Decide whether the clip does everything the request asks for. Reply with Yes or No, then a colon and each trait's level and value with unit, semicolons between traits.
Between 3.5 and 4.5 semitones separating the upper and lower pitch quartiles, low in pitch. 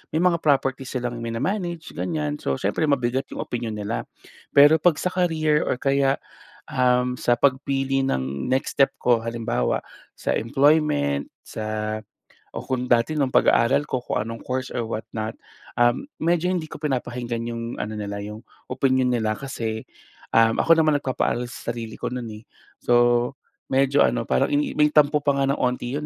Yes: average, 3.8 semitones; low, 125 Hz